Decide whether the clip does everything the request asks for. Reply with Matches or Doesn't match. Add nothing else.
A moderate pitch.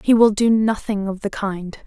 Doesn't match